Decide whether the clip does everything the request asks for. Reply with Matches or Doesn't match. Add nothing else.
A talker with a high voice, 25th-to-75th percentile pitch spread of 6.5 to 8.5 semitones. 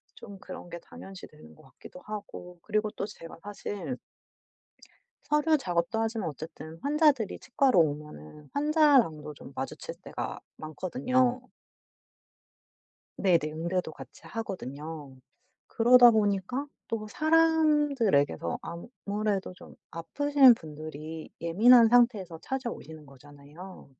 Matches